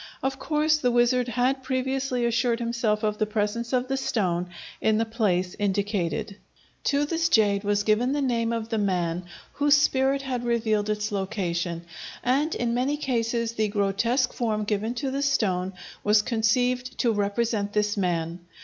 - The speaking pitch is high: Yes, high, 230 Hz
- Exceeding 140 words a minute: Yes, average, 165 wpm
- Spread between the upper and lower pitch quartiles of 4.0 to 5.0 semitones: No, average, 3.6 semitones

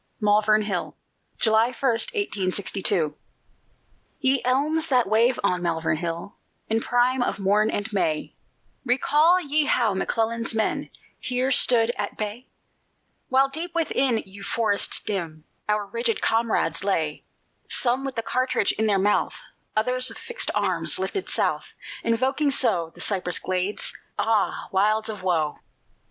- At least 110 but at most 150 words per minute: Yes, slow, 135 wpm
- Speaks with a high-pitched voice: Yes, high, 220 Hz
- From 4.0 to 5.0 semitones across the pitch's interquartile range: Yes, average, 4.5 semitones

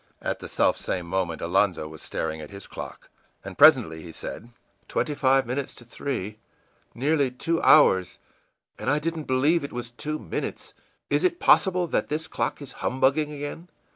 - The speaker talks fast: No, average, 175 wpm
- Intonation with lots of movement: Yes, wide, 8.1 semitones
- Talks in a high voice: No, low, 130 Hz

